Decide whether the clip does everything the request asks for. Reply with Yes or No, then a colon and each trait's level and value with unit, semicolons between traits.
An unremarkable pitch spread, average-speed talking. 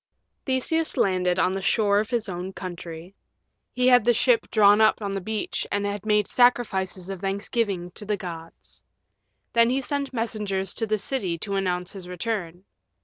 Yes: average, 3.6 semitones; average, 175 wpm